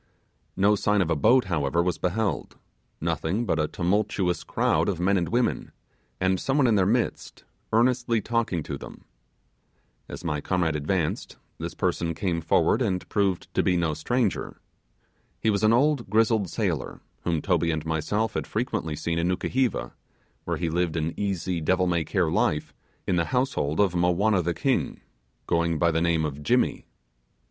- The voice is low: Yes, very low, 90 Hz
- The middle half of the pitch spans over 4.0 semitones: Yes, average, 4.7 semitones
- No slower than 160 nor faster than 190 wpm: Yes, average, 170 wpm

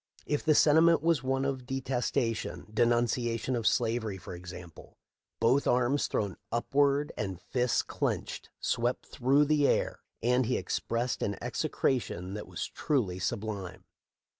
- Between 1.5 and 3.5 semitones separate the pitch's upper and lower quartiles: No, average, 3.9 semitones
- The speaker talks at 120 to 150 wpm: Yes, average, 145 wpm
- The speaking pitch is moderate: No, low, 120 Hz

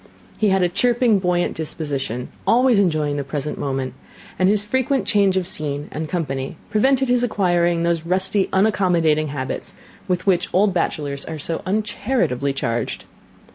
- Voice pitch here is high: No, medium, 175 Hz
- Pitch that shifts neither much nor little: No, wide, 5.7 semitones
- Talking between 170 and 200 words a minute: No, average, 150 wpm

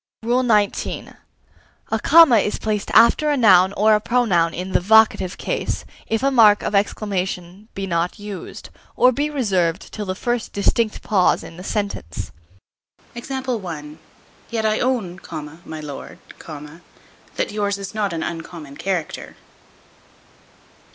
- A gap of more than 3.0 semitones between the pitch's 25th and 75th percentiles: Yes, average, 4.1 semitones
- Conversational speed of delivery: No, slow, 130 wpm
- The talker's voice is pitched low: No, high, 205 Hz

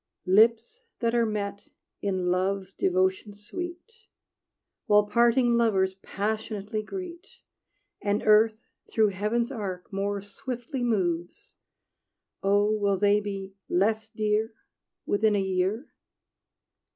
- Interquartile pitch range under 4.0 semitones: Yes, average, 2.8 semitones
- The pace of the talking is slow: Yes, slow, 105 wpm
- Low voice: No, high, 210 Hz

